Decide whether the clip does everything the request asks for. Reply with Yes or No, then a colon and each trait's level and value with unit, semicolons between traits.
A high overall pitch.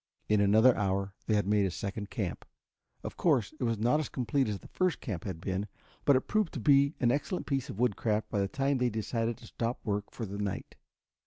No: low, 110 Hz